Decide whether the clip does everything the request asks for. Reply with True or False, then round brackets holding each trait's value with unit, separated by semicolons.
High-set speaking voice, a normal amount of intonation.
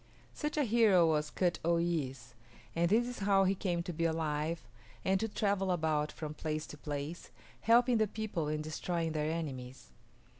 False (170 Hz; 4.4 semitones)